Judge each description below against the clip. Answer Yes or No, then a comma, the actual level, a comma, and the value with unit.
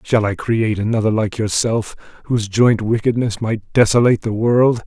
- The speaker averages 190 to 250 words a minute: No, average, 160 wpm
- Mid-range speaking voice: No, low, 110 Hz